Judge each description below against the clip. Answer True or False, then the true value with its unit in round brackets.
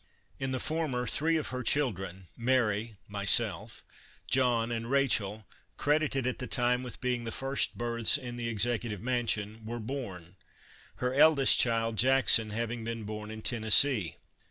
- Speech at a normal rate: True (150 wpm)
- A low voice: True (120 Hz)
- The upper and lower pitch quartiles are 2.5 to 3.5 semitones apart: True (2.9 semitones)